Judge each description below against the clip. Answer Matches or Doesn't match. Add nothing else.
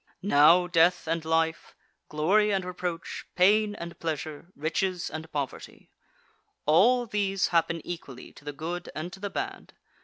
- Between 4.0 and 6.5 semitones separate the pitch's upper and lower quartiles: Doesn't match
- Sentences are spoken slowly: Doesn't match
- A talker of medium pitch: Matches